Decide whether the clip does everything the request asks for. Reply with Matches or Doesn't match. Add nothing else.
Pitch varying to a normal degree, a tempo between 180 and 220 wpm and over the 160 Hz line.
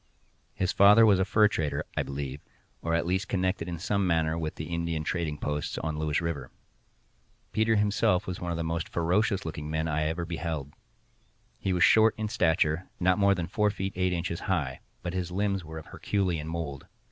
Doesn't match